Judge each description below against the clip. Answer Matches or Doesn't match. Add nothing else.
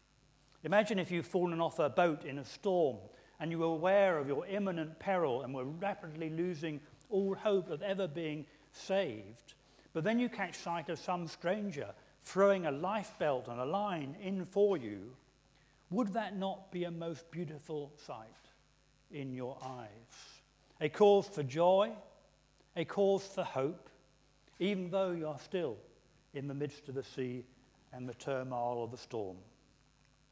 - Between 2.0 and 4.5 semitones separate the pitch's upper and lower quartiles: Doesn't match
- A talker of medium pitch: Matches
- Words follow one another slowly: Doesn't match